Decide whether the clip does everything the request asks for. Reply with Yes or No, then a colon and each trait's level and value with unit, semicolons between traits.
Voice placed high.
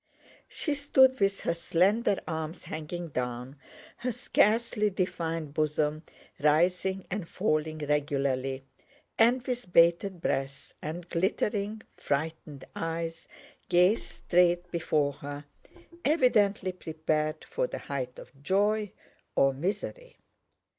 No: medium, 170 Hz